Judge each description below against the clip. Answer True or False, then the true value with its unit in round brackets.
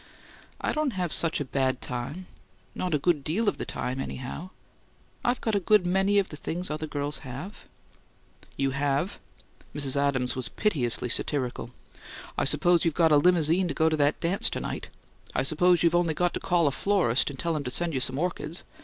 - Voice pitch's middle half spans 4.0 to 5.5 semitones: True (4.5 semitones)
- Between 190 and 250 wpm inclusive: True (205 wpm)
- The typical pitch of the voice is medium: True (155 Hz)